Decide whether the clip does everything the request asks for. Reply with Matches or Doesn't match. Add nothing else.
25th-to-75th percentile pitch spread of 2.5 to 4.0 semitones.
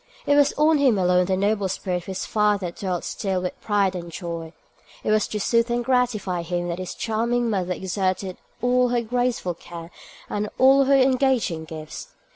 Doesn't match